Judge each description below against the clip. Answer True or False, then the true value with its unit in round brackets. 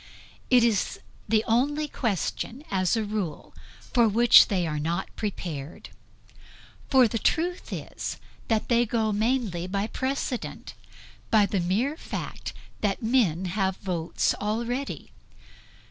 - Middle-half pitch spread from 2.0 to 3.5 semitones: False (4.3 semitones)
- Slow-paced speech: True (125 wpm)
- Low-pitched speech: False (215 Hz)